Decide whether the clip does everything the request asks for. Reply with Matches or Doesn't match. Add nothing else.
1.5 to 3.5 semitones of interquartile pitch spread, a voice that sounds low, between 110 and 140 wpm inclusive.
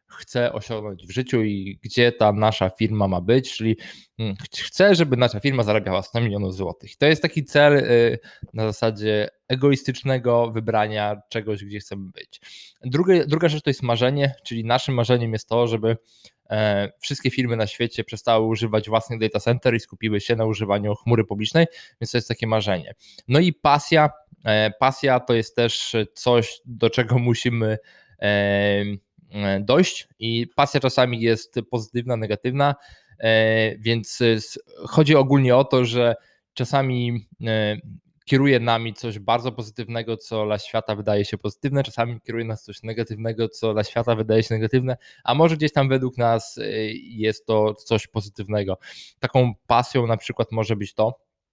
Doesn't match